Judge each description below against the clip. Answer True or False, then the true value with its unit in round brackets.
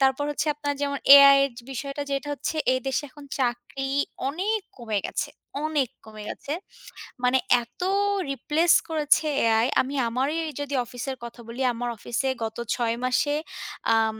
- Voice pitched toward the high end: True (270 Hz)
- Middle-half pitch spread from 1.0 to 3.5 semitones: True (3.2 semitones)